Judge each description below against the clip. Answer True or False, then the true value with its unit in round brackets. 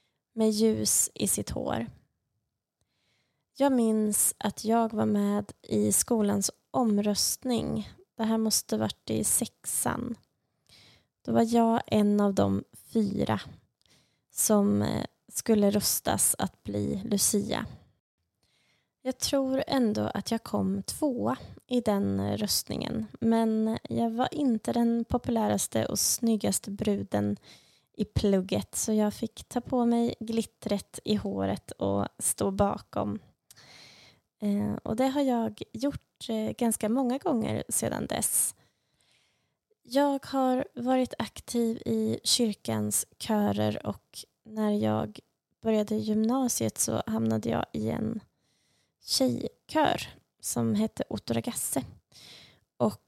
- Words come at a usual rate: False (110 wpm)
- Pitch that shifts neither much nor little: True (4.4 semitones)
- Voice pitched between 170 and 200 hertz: False (215 Hz)